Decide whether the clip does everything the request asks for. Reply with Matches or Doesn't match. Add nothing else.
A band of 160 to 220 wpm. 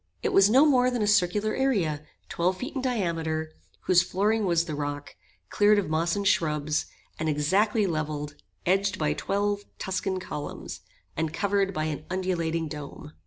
Matches